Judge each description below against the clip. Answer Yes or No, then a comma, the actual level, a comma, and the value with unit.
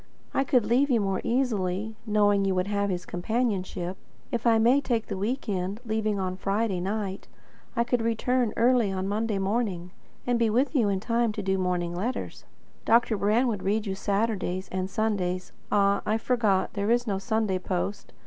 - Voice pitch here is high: Yes, high, 210 Hz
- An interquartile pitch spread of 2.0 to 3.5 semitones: Yes, average, 3.2 semitones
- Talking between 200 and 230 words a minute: No, average, 185 wpm